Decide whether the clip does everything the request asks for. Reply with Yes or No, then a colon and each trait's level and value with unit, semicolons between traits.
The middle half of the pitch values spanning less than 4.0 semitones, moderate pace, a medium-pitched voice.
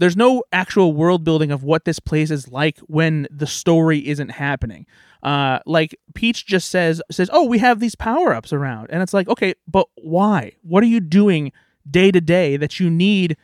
No: average, 4.3 semitones; average, 195 wpm; medium, 170 Hz